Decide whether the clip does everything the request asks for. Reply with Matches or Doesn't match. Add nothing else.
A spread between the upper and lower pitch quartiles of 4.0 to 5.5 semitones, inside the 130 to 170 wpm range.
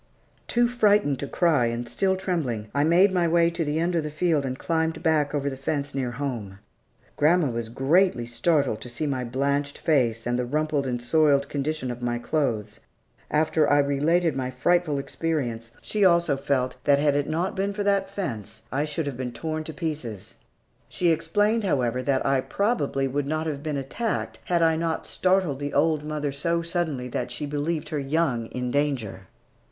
Doesn't match